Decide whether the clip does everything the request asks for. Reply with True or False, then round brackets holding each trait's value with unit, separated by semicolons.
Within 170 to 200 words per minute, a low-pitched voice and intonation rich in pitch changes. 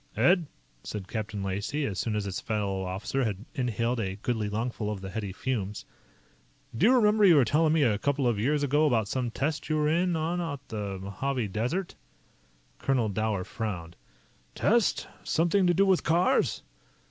True (180 wpm; 120 Hz; 7.0 semitones)